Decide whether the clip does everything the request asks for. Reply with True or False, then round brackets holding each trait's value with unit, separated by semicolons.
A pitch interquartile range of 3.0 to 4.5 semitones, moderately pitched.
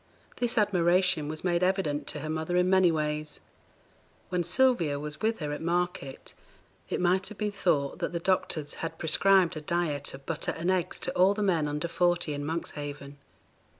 True (3.6 semitones; 170 Hz)